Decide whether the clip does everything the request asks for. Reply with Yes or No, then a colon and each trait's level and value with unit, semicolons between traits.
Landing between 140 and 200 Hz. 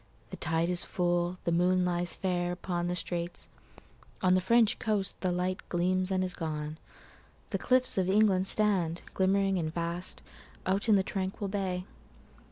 Yes: medium, 185 Hz